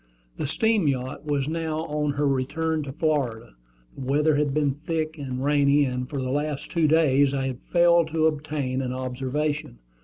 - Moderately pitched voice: Yes, medium, 145 Hz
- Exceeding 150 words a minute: Yes, average, 180 wpm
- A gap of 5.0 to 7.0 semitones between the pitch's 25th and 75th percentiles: No, average, 2.7 semitones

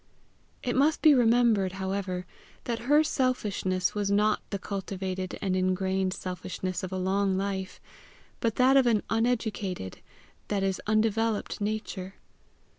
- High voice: Yes, high, 200 Hz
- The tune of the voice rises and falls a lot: No, average, 3.3 semitones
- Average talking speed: No, slow, 130 wpm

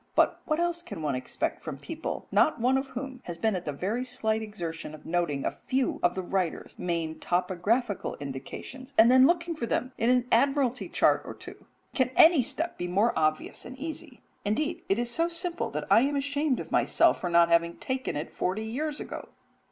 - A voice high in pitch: Yes, high, 235 Hz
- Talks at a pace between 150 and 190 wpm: No, fast, 205 wpm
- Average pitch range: No, wide, 7.7 semitones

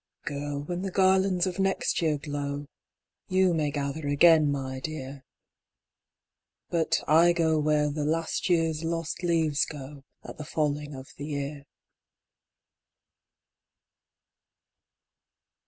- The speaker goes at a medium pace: No, slow, 115 wpm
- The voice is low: No, medium, 155 Hz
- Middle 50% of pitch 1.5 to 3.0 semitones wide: Yes, narrow, 2.6 semitones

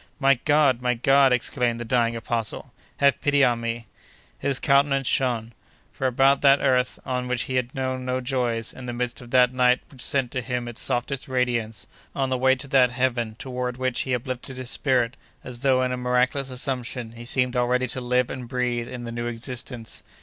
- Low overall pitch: Yes, low, 125 Hz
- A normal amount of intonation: No, narrow, 1.5 semitones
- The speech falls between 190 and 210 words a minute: Yes, average, 200 wpm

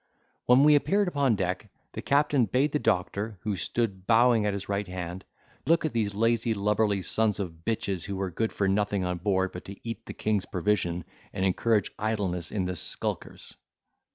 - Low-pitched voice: Yes, low, 105 Hz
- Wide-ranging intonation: No, average, 3.4 semitones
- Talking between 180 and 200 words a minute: Yes, average, 185 wpm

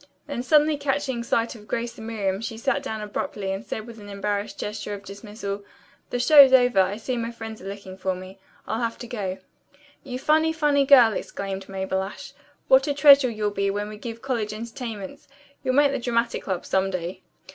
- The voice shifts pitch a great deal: No, average, 4.3 semitones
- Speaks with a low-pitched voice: No, high, 225 Hz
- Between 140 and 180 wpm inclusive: No, average, 200 wpm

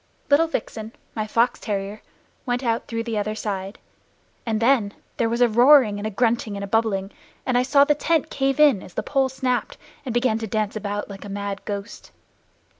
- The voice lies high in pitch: Yes, high, 225 Hz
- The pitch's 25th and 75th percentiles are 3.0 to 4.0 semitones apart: Yes, average, 3.5 semitones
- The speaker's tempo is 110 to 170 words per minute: No, average, 195 wpm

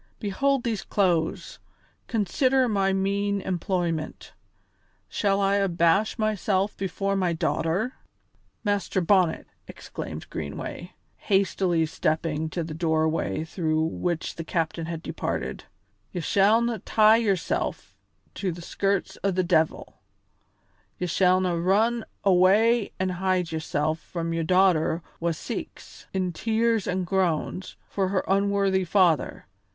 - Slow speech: Yes, slow, 120 wpm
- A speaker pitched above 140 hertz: Yes, medium, 185 Hz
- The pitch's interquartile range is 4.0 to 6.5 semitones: No, average, 3.2 semitones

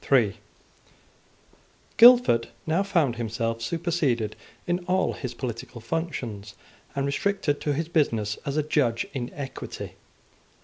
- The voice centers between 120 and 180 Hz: Yes, medium, 140 Hz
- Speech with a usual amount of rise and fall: No, wide, 6.2 semitones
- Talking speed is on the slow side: Yes, slow, 115 wpm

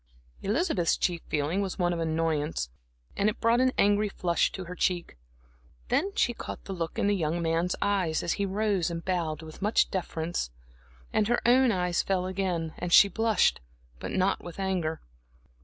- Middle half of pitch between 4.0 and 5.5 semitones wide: No, average, 3.4 semitones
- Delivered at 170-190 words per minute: Yes, average, 180 wpm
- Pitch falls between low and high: Yes, medium, 180 Hz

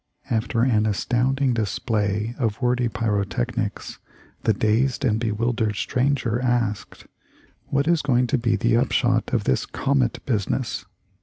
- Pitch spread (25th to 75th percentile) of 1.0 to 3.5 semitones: Yes, average, 2.8 semitones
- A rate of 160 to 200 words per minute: No, slow, 135 wpm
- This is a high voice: No, low, 120 Hz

